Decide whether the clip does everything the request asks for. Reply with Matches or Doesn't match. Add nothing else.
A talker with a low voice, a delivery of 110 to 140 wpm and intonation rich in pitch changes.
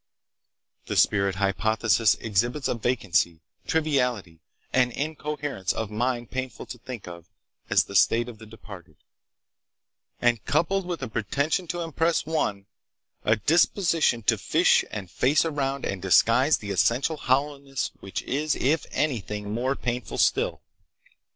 Matches